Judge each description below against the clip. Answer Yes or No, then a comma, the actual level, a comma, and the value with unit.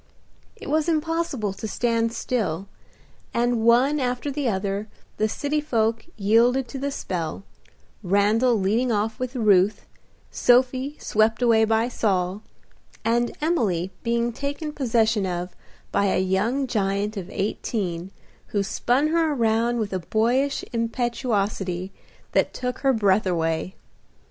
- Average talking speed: No, slow, 130 wpm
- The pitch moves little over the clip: No, average, 4.2 semitones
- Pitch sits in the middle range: No, high, 225 Hz